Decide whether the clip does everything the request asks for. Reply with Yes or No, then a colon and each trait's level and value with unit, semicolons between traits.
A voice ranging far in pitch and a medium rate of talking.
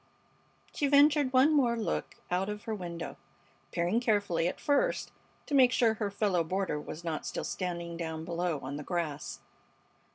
Yes: wide, 6.1 semitones; average, 165 wpm